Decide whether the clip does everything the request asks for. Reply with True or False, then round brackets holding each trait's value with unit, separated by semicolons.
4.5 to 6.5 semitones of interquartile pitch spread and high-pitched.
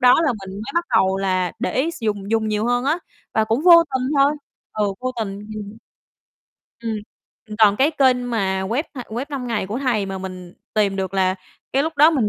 True (4.8 semitones; 225 Hz)